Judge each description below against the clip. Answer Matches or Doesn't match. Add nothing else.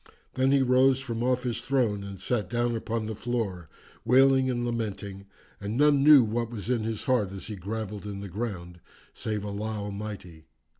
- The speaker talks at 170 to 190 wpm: Matches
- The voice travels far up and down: Doesn't match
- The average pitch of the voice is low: Matches